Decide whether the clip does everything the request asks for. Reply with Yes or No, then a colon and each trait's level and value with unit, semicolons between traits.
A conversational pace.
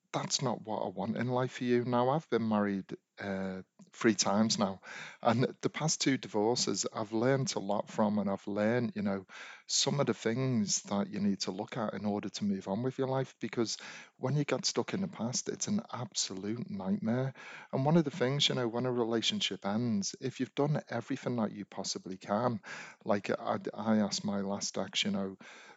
No: fast, 210 wpm